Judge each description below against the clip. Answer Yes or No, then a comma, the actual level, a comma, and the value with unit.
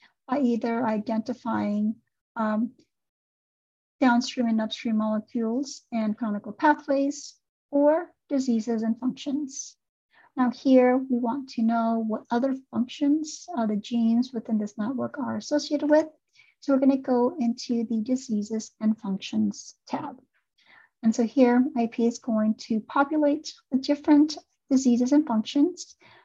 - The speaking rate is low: Yes, slow, 130 wpm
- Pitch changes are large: No, average, 4.1 semitones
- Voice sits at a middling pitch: No, high, 245 Hz